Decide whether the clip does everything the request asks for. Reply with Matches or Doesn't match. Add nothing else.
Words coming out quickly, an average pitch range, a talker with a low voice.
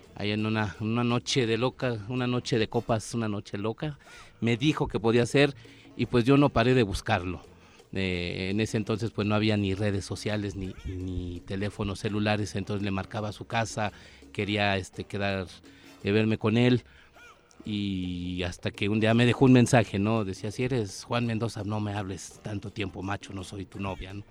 Matches